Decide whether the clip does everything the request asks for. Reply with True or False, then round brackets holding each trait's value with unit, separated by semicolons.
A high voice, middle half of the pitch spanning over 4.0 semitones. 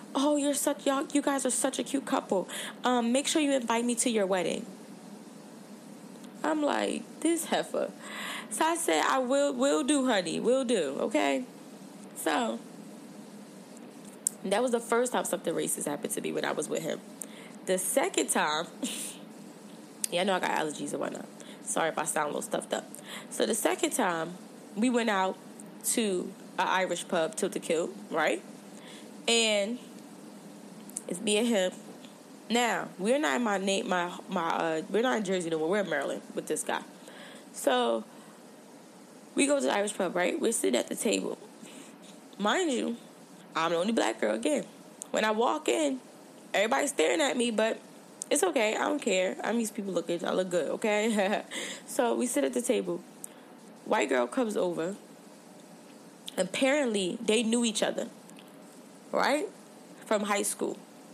True (235 Hz; 4.6 semitones)